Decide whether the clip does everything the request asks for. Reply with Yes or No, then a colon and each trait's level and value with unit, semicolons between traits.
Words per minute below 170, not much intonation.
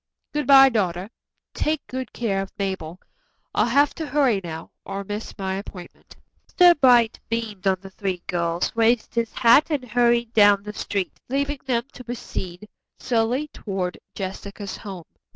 No: average, 155 wpm; average, 4.5 semitones